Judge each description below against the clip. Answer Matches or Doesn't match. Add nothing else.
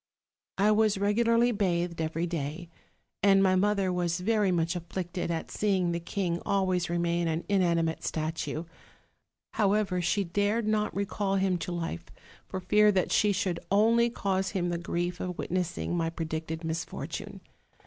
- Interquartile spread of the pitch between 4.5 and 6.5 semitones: Doesn't match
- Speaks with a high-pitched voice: Doesn't match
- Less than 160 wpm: Matches